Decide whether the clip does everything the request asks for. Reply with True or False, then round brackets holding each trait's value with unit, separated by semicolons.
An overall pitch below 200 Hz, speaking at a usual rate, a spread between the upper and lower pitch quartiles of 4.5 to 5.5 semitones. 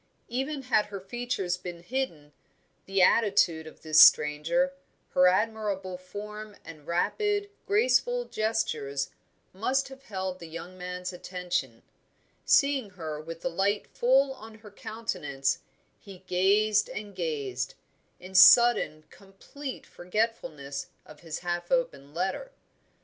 False (190 Hz; 120 wpm; 5.2 semitones)